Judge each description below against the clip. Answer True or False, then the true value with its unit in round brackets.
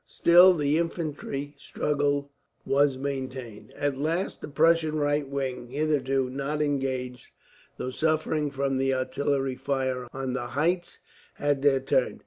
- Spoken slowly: True (130 wpm)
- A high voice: False (140 Hz)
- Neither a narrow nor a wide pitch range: False (2.2 semitones)